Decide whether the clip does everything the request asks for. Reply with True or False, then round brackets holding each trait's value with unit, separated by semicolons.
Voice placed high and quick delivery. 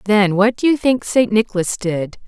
True (210 Hz; 210 wpm)